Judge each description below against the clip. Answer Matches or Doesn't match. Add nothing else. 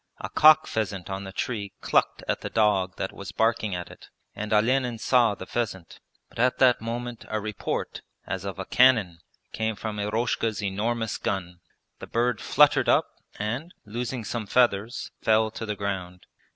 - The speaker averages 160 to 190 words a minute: Matches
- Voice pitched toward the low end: Matches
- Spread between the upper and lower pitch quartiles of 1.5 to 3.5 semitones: Matches